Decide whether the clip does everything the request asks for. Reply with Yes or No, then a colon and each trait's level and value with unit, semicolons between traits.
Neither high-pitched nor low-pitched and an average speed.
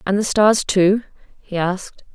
No: high, 195 Hz; average, 170 wpm